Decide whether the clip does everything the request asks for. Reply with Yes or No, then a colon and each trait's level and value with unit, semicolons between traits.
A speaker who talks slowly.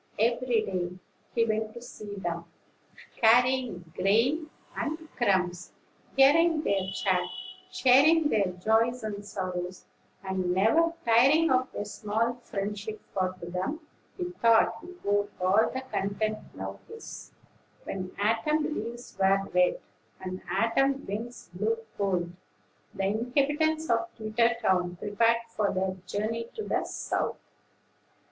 Yes: slow, 125 wpm